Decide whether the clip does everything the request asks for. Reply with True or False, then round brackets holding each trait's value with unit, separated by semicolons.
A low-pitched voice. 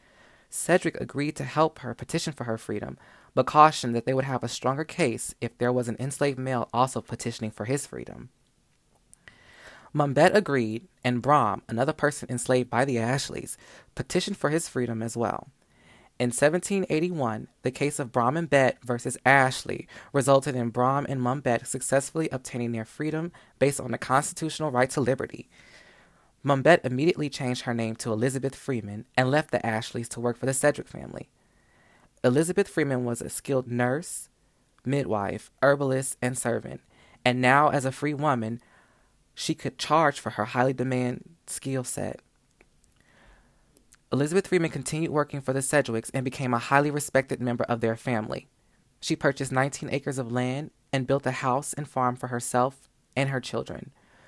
True (130 Hz)